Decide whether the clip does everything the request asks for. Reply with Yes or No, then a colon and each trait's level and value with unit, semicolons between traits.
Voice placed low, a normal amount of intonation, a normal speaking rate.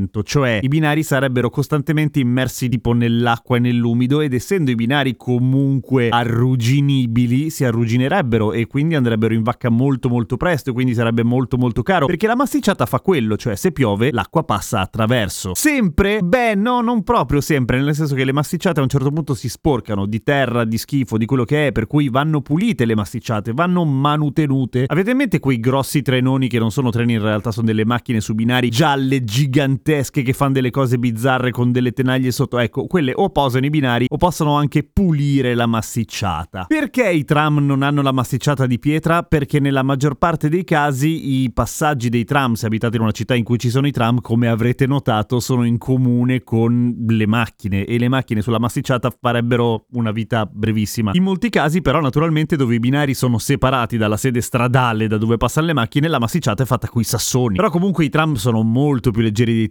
No: low, 130 Hz; average, 3.7 semitones; fast, 200 wpm